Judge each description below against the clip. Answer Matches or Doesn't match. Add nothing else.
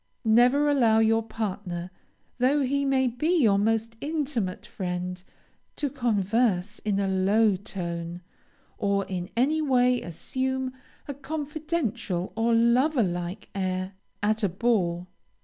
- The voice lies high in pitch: Matches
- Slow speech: Matches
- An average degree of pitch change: Doesn't match